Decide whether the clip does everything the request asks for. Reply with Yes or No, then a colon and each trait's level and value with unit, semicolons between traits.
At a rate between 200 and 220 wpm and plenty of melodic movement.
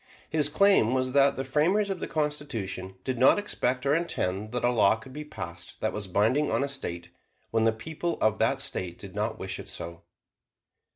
Yes: fast, 205 wpm; wide, 6.6 semitones